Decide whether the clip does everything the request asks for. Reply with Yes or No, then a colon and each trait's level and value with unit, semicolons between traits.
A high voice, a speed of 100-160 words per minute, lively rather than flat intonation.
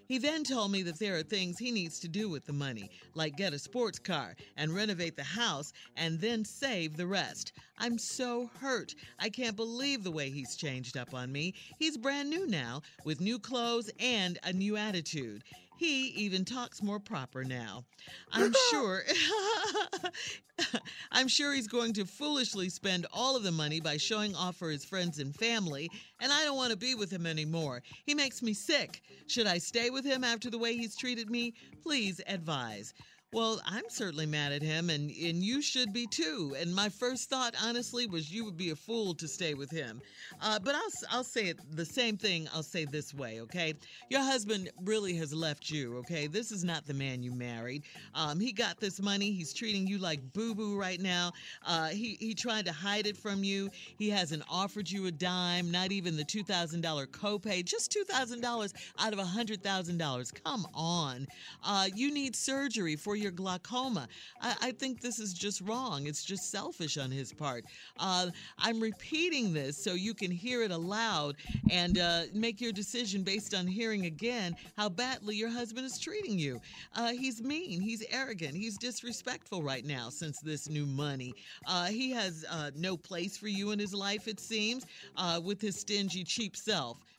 No: high, 195 Hz; average, 195 wpm; wide, 6.2 semitones